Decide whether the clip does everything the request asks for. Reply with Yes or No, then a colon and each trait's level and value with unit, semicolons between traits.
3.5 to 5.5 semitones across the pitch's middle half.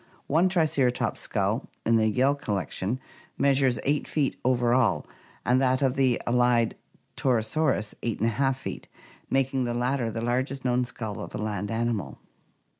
No: average, 2.8 semitones